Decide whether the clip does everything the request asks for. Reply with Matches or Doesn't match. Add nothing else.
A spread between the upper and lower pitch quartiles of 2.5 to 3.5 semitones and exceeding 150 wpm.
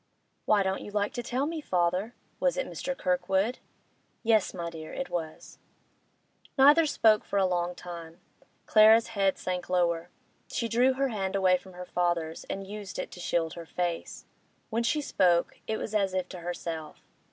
Doesn't match